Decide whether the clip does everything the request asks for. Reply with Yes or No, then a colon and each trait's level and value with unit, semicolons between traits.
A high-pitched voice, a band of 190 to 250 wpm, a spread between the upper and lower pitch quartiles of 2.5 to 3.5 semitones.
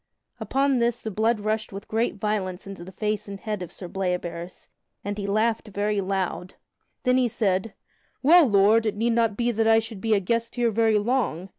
Yes: high, 215 Hz; average, 200 wpm; average, 2.8 semitones